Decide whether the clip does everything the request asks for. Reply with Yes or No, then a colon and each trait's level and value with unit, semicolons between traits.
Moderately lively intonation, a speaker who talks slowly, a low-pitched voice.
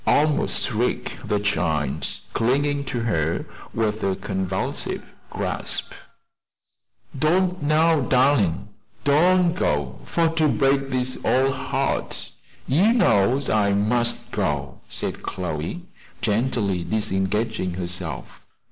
No: wide, 7.0 semitones; slow, 105 wpm; low, 115 Hz